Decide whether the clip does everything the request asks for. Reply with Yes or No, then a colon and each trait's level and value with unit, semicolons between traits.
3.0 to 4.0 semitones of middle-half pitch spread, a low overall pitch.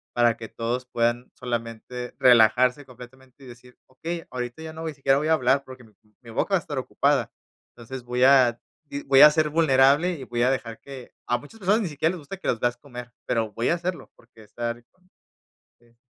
Yes: average, 3.4 semitones; low, 125 Hz